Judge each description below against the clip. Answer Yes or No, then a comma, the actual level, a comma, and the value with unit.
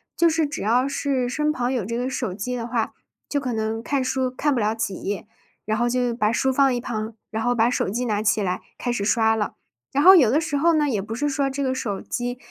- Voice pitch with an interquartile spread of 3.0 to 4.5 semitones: Yes, average, 3.5 semitones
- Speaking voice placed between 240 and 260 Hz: Yes, high, 245 Hz